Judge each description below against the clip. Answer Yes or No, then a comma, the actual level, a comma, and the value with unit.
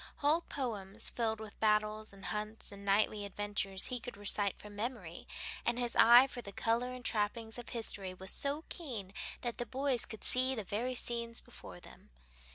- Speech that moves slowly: No, average, 180 wpm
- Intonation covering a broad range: No, average, 3.1 semitones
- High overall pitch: Yes, high, 220 Hz